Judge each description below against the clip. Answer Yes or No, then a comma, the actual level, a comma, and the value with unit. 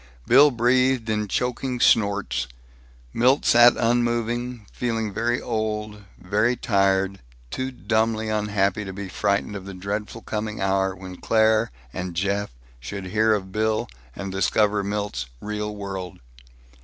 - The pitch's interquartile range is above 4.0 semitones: No, average, 2.8 semitones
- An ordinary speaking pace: No, slow, 130 wpm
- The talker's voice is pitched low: Yes, low, 105 Hz